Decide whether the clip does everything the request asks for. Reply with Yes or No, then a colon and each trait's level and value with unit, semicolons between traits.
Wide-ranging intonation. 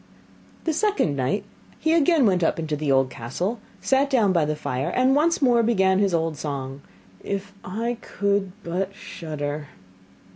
Yes: wide, 7.9 semitones